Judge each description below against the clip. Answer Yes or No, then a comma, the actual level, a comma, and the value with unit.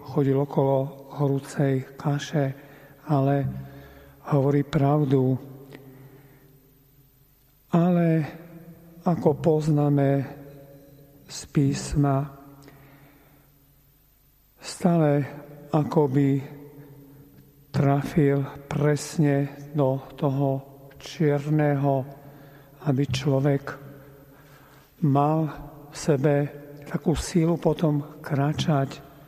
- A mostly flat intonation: Yes, narrow, 1.1 semitones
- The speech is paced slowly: Yes, slow, 60 wpm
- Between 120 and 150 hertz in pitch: Yes, medium, 140 Hz